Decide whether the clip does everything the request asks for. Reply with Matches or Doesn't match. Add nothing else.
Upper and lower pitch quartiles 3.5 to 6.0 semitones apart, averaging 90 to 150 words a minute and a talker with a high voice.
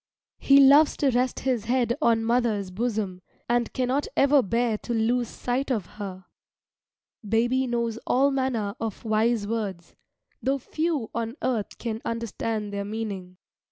Doesn't match